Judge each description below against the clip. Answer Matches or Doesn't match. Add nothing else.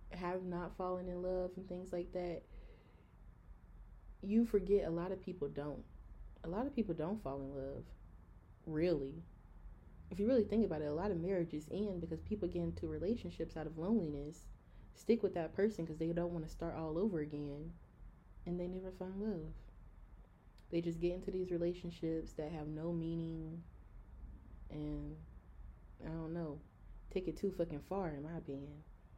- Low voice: Doesn't match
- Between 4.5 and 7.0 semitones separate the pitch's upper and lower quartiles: Doesn't match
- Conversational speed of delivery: Matches